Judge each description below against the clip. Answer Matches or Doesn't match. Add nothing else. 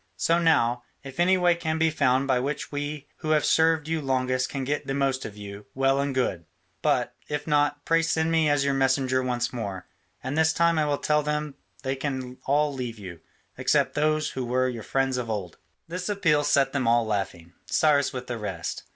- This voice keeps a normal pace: Doesn't match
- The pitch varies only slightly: Doesn't match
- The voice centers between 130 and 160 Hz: Matches